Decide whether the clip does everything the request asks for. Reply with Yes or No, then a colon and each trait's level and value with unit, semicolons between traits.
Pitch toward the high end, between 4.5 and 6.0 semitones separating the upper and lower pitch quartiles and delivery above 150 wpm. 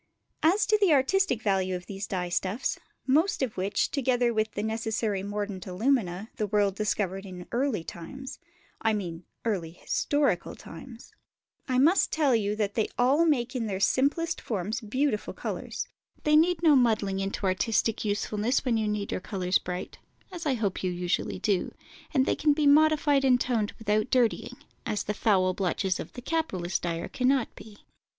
Yes: high, 220 Hz; wide, 5.5 semitones; average, 170 wpm